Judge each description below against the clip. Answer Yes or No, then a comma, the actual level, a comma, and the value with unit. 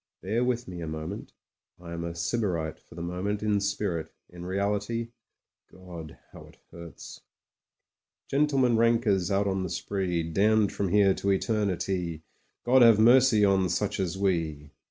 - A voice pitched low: Yes, very low, 95 Hz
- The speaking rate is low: No, average, 165 wpm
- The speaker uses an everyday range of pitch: Yes, average, 3.8 semitones